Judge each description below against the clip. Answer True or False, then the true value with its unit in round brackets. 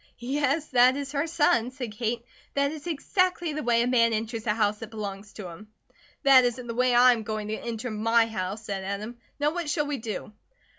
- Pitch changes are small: False (4.4 semitones)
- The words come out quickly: True (215 wpm)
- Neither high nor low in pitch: False (240 Hz)